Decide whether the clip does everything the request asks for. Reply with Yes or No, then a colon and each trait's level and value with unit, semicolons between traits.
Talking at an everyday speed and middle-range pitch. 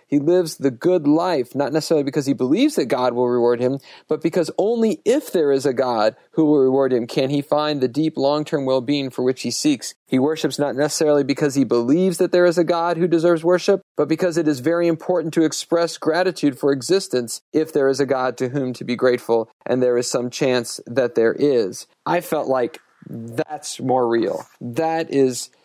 No: fast, 215 wpm; medium, 150 Hz